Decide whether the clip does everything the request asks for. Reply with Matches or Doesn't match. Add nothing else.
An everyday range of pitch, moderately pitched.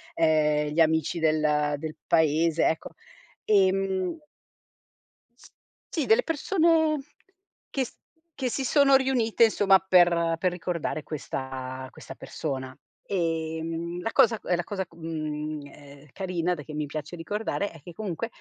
Matches